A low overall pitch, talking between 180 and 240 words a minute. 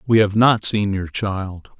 Yes: low, 100 Hz; average, 200 wpm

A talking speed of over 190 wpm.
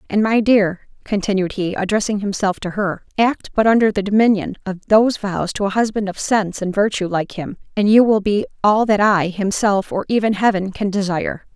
Yes: average, 200 wpm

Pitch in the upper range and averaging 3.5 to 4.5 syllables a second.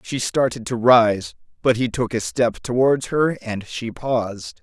No: low, 120 Hz; 4.0 syllables/s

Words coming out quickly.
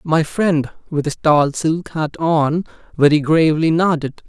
No: average, 155 wpm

